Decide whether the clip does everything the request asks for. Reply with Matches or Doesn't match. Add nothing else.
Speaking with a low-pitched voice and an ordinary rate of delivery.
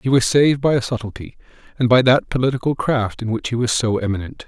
Doesn't match